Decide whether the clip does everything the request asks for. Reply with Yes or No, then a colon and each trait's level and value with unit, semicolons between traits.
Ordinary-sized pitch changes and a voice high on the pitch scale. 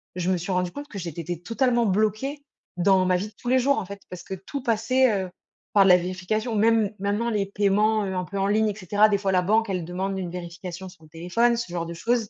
Yes: average, 3.4 semitones; high, 195 Hz